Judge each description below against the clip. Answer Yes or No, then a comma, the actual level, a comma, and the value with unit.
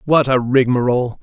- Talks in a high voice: No, low, 130 Hz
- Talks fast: No, average, 145 wpm